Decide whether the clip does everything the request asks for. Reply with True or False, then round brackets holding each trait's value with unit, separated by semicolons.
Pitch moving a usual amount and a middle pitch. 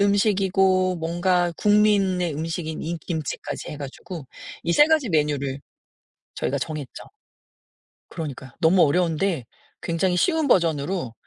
True (3.9 semitones; 175 Hz)